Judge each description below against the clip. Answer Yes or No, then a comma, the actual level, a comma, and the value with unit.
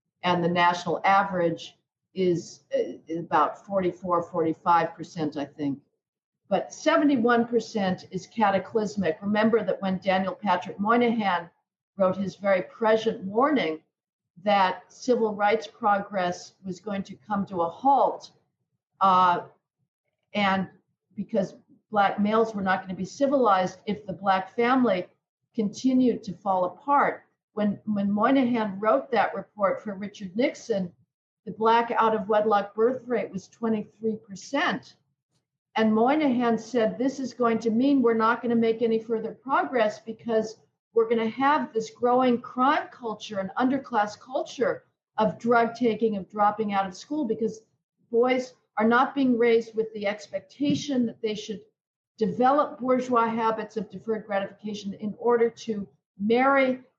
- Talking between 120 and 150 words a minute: Yes, average, 140 wpm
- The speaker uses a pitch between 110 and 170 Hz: No, high, 215 Hz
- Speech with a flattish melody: No, average, 3.7 semitones